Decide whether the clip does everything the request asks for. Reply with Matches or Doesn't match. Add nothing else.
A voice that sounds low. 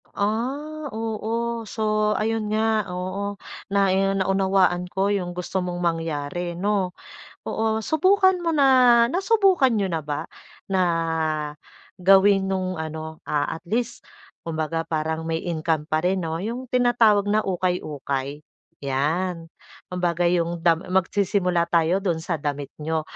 Doesn't match